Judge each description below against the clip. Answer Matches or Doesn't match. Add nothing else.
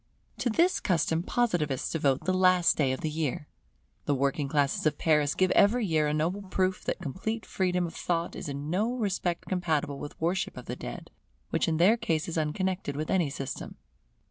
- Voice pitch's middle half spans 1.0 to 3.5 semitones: Doesn't match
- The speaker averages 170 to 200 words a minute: Matches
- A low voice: Doesn't match